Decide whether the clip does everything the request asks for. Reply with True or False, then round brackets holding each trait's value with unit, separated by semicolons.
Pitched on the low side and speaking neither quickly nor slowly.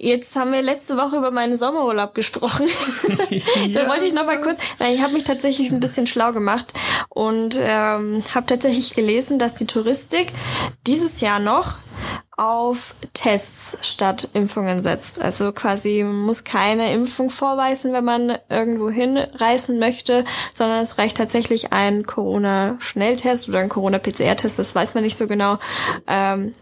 False (235 Hz; 150 wpm)